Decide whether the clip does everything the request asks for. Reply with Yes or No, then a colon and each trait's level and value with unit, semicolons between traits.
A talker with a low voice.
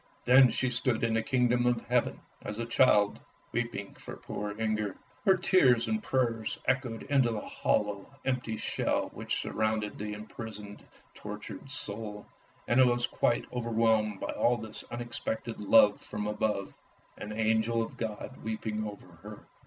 Yes: low, 115 Hz